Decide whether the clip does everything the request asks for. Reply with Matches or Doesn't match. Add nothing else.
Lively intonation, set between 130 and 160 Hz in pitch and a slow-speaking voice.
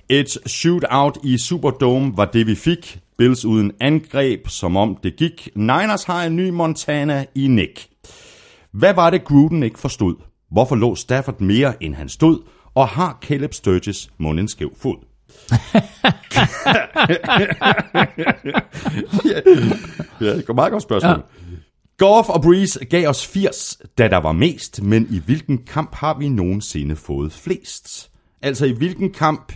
Matches